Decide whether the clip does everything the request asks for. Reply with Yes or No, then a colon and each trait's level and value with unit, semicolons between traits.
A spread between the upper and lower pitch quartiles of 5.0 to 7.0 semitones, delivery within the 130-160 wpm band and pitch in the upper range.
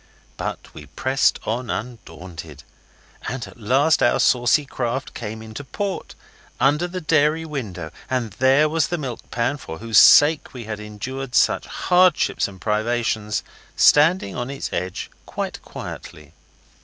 No: wide, 5.5 semitones; average, 145 wpm; low, 125 Hz